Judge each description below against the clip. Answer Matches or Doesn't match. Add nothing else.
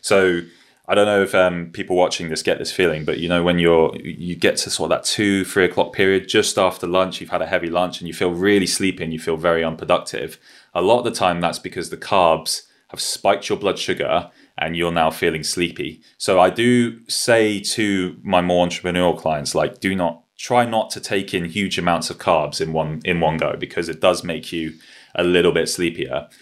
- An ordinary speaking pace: Doesn't match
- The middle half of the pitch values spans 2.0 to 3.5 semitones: Matches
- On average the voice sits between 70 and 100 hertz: Matches